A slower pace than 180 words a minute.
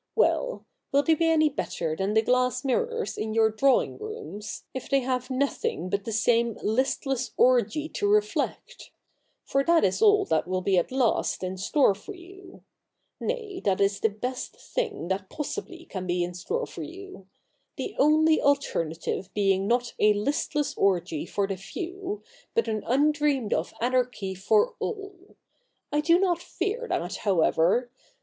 Yes: average, 165 wpm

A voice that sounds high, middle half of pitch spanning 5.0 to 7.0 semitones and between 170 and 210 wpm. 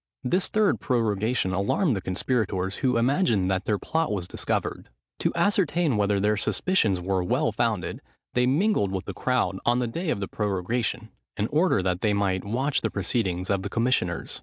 No: low, 110 Hz; wide, 5.4 semitones; average, 175 wpm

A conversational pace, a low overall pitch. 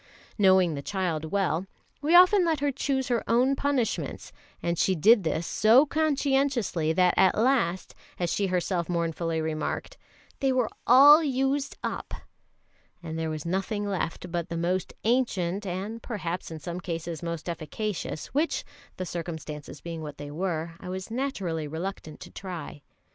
No: average, 155 wpm; medium, 185 Hz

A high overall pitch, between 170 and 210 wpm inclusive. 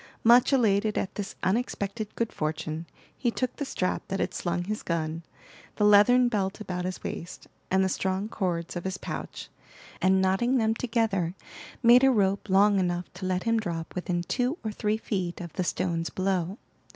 Yes: high, 195 Hz; average, 180 wpm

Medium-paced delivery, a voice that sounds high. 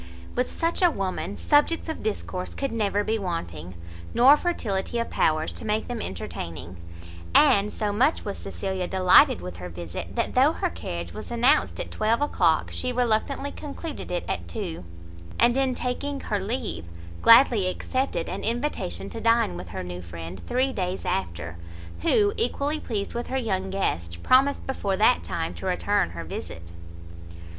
Yes: average, 165 wpm; high, 205 Hz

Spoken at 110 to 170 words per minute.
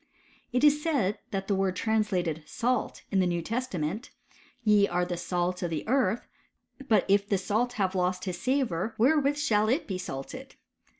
No: average, 190 wpm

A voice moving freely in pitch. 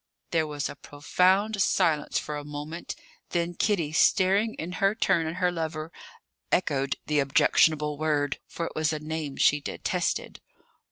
No: average, 3.1 semitones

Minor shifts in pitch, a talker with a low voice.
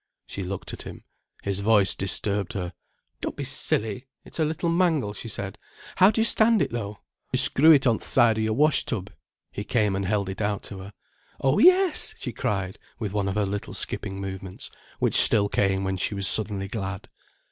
No: average, 4.2 semitones; low, 105 Hz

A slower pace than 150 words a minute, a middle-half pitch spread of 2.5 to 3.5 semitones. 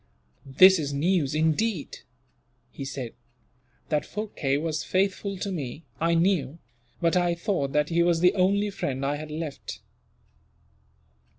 No: slow, 135 wpm; average, 4.3 semitones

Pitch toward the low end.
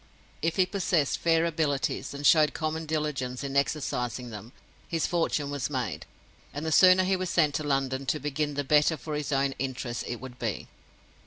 No: medium, 145 Hz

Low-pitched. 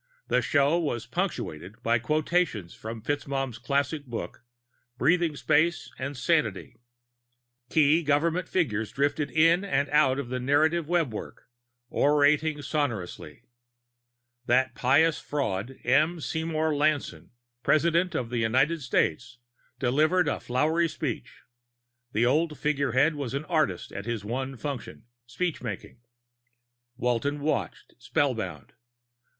No: medium, 145 Hz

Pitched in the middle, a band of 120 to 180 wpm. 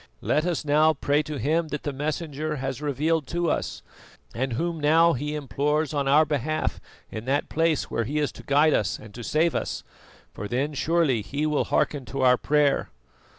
No: medium, 150 Hz; average, 195 wpm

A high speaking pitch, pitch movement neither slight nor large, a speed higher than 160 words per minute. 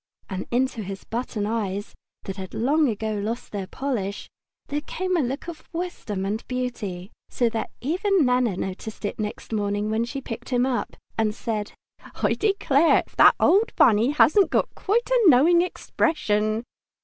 No: high, 235 Hz; wide, 6.0 semitones; average, 170 wpm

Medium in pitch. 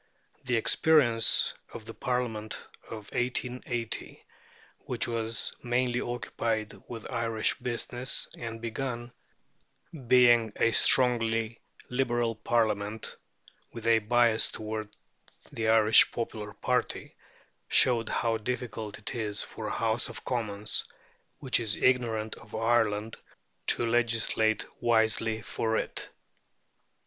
No: low, 115 Hz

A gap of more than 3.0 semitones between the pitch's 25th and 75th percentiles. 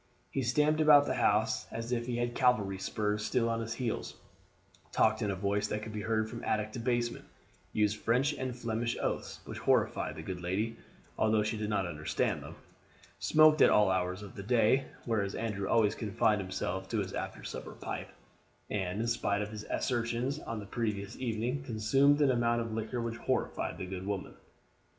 No: average, 2.7 semitones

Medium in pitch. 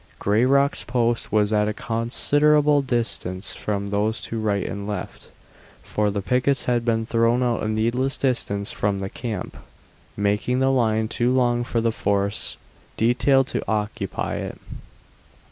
No: low, 115 Hz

